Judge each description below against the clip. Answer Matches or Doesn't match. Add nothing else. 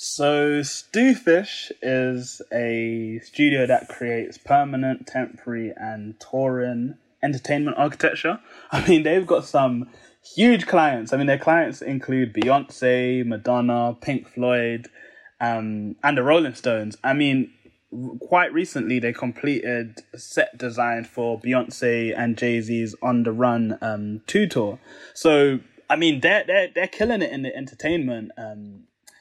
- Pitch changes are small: Doesn't match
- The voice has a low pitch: Matches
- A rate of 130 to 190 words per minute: Matches